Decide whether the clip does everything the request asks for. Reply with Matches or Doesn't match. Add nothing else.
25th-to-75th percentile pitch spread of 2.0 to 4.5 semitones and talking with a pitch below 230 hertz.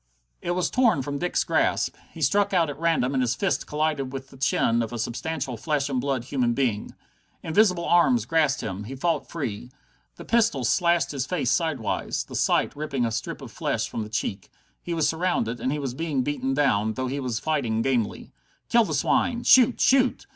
Doesn't match